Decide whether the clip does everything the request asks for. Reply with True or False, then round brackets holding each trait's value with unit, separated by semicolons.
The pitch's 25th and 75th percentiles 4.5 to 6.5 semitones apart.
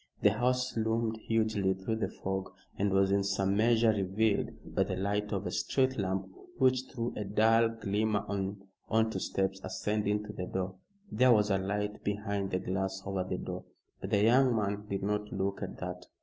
False (2.4 semitones)